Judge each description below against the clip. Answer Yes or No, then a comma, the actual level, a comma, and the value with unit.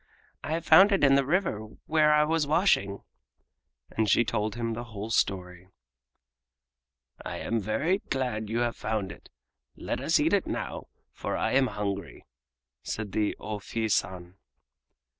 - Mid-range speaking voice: No, low, 115 Hz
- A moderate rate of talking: Yes, average, 160 wpm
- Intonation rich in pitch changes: Yes, wide, 6.1 semitones